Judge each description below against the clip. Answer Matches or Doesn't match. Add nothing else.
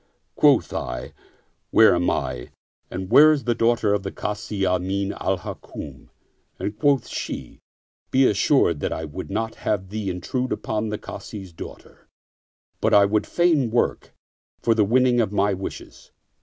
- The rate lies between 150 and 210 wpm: Matches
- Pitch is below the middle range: Matches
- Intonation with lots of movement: Doesn't match